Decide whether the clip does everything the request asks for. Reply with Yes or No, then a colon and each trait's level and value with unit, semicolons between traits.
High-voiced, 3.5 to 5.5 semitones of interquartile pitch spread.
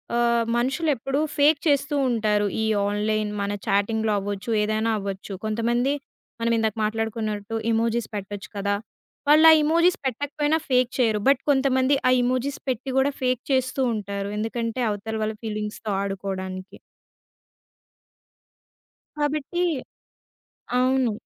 Yes: high, 230 Hz; average, 4.2 semitones